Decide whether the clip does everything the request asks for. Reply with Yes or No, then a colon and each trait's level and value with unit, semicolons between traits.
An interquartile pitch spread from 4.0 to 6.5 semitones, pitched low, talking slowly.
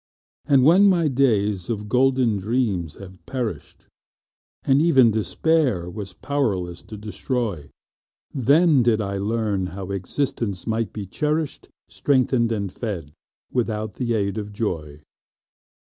Yes: average, 5.0 semitones; low, 110 Hz; slow, 125 wpm